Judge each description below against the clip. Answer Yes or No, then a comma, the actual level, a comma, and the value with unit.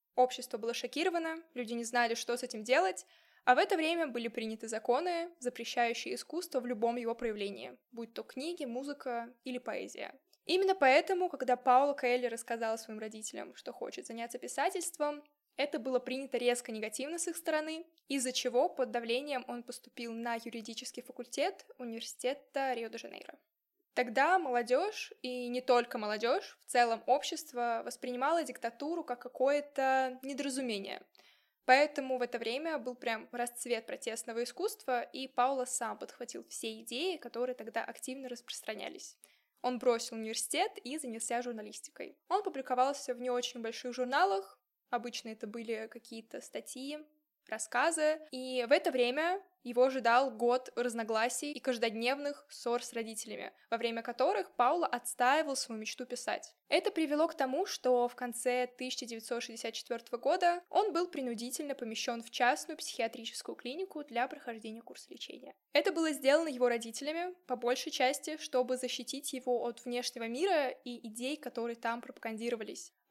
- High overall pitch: Yes, very high, 250 Hz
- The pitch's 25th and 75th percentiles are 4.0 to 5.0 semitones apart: No, average, 3.4 semitones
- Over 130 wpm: Yes, average, 145 wpm